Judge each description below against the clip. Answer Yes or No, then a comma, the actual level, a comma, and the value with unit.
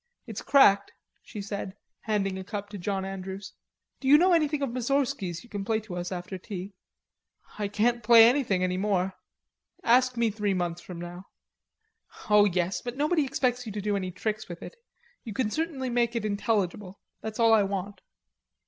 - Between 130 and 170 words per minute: No, average, 185 wpm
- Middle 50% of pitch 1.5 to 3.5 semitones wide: No, average, 4.0 semitones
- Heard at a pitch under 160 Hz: No, high, 210 Hz